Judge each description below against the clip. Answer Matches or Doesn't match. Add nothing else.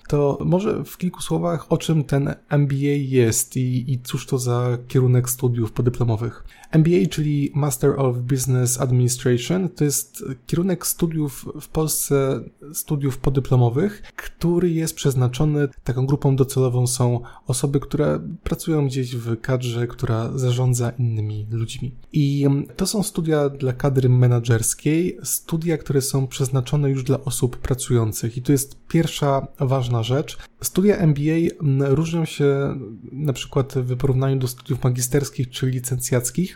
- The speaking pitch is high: Doesn't match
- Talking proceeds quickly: Doesn't match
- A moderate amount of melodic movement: Matches